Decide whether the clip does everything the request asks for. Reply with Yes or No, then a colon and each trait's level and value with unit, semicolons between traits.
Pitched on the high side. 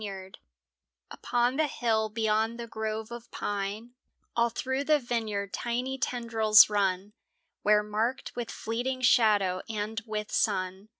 Yes: high, 220 Hz